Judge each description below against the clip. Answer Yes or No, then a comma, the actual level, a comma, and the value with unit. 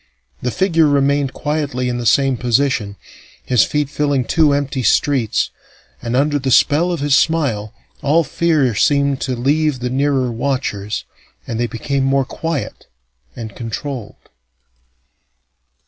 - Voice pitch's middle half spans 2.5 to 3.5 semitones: Yes, average, 3.0 semitones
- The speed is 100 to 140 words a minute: Yes, slow, 135 wpm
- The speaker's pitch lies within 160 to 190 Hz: No, low, 135 Hz